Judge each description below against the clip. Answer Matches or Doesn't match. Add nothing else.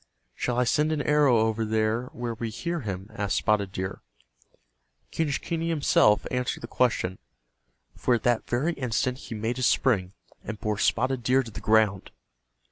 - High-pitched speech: Doesn't match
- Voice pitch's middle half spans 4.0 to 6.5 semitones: Doesn't match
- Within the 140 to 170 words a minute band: Matches